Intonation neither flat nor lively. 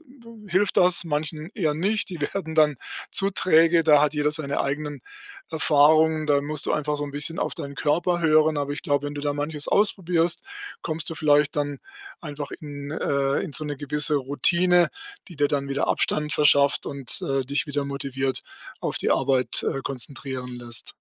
No: narrow, 2.3 semitones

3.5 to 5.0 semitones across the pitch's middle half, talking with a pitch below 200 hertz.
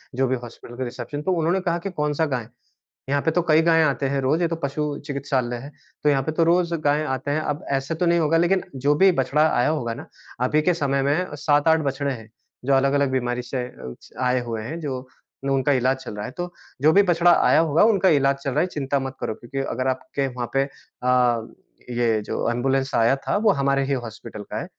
Yes: average, 3.8 semitones; medium, 140 Hz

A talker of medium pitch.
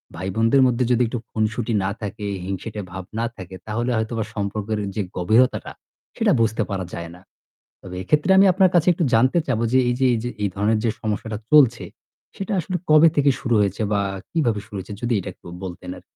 No: low, 110 Hz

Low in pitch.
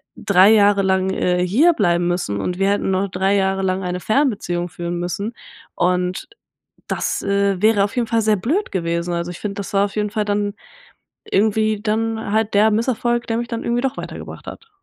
No: high, 200 Hz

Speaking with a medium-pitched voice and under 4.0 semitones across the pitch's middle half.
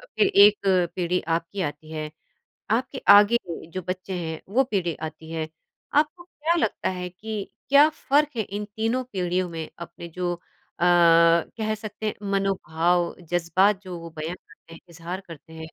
No: medium, 180 Hz; average, 4.3 semitones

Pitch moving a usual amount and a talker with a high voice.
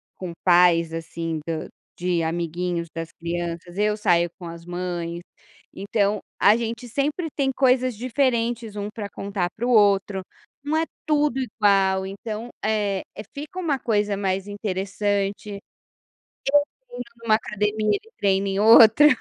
Yes: average, 4.6 semitones; high, 205 Hz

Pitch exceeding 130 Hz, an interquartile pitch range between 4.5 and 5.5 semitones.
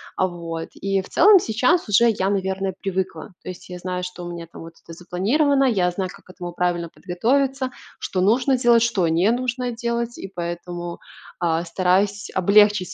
Yes: high, 190 Hz; average, 5.0 semitones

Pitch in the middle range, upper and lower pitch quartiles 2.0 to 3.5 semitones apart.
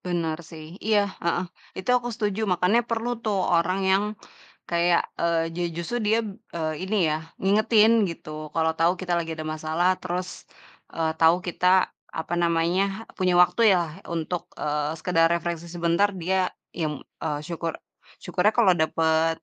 Yes: medium, 170 Hz; narrow, 2.4 semitones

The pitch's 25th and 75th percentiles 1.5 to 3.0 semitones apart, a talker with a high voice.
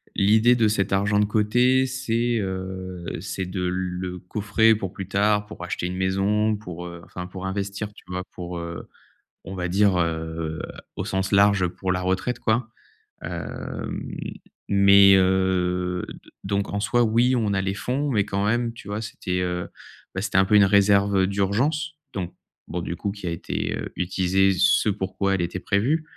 No: narrow, 2.5 semitones; low, 100 Hz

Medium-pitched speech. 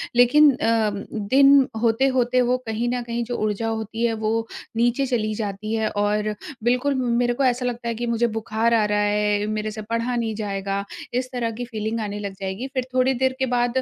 No: high, 230 Hz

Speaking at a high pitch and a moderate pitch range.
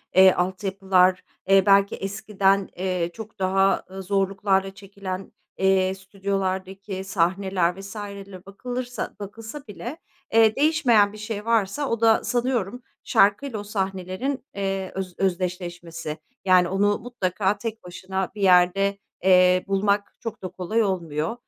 No: high, 195 Hz; narrow, 2.0 semitones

